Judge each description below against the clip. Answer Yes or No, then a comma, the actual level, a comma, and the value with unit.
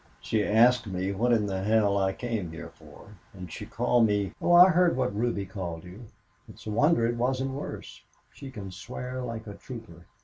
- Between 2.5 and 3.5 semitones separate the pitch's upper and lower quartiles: No, average, 4.3 semitones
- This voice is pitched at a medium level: No, low, 110 Hz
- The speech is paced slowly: No, fast, 205 wpm